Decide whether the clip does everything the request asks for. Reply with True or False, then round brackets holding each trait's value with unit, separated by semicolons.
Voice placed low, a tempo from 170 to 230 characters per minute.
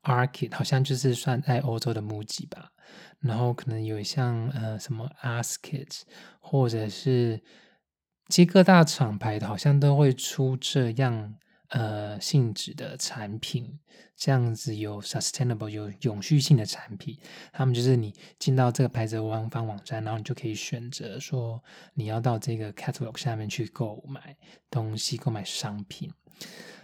False (125 Hz; 275 characters per minute)